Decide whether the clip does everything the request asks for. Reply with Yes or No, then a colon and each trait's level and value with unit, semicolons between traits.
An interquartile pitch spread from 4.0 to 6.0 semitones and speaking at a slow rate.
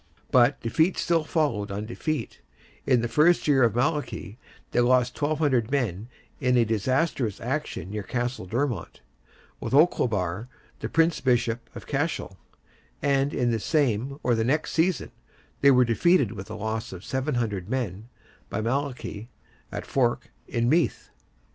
No: average, 4.3 semitones; average, 150 wpm